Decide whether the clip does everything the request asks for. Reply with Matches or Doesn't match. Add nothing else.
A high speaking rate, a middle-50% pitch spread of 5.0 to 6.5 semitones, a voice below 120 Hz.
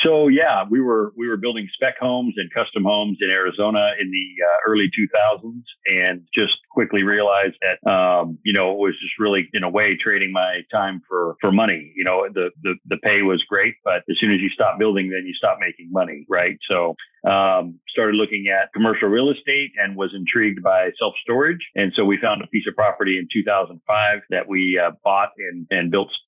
Doesn't match